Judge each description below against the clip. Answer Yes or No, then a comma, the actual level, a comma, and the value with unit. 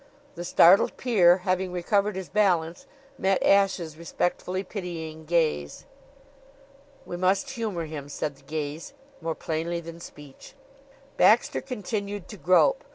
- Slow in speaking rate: Yes, slow, 125 wpm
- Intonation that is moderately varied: Yes, average, 3.7 semitones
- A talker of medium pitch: Yes, medium, 175 Hz